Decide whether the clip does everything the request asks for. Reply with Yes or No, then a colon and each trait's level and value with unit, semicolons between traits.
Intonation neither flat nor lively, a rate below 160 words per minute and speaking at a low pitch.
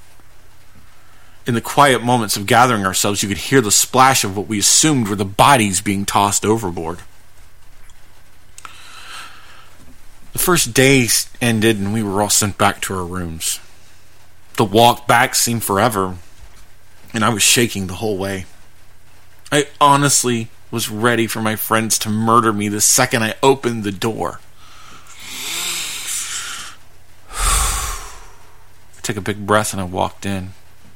Yes: average, 3.4 semitones; average, 140 wpm; low, 105 Hz